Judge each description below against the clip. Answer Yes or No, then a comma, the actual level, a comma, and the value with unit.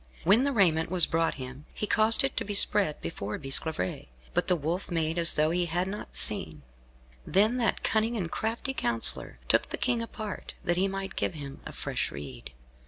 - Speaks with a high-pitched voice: No, medium, 175 Hz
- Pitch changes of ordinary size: No, wide, 5.8 semitones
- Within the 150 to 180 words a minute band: No, average, 195 wpm